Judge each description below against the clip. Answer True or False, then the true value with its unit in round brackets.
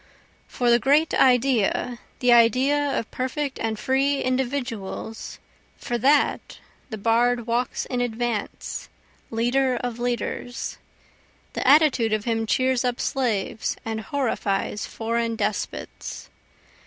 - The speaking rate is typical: False (115 wpm)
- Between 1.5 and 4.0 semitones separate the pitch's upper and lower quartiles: True (2.6 semitones)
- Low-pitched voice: False (245 Hz)